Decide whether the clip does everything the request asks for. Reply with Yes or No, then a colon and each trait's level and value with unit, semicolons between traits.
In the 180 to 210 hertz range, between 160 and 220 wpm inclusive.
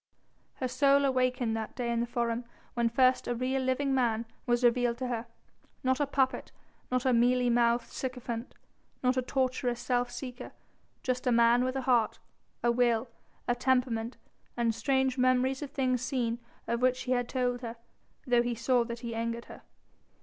No: high, 245 Hz; average, 180 wpm